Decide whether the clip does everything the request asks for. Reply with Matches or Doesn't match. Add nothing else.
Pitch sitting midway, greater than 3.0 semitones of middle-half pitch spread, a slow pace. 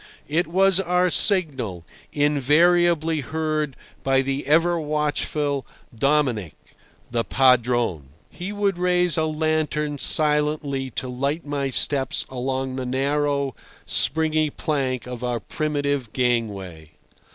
Matches